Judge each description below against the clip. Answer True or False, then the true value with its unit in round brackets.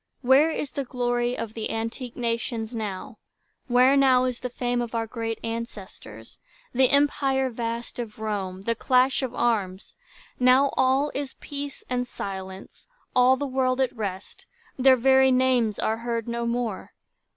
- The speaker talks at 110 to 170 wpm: True (150 wpm)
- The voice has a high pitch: True (245 Hz)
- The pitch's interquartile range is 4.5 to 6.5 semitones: False (2.4 semitones)